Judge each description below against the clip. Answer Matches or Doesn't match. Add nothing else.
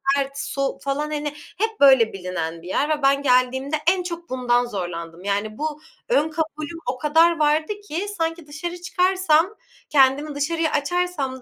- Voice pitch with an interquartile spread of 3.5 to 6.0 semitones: Matches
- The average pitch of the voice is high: Matches